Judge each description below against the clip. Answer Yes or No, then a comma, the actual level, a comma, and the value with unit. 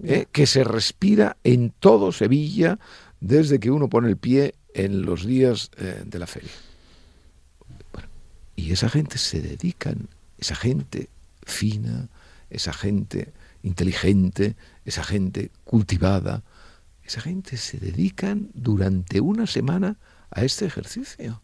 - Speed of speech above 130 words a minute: No, slow, 125 wpm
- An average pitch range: No, wide, 6.7 semitones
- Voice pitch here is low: Yes, low, 105 Hz